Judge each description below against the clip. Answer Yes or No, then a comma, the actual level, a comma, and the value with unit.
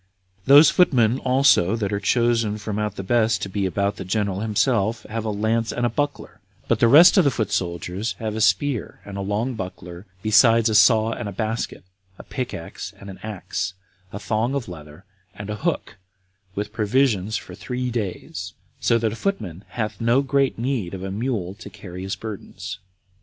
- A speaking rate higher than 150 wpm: Yes, average, 195 wpm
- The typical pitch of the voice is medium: No, low, 110 Hz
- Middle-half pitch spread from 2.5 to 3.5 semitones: Yes, average, 3.2 semitones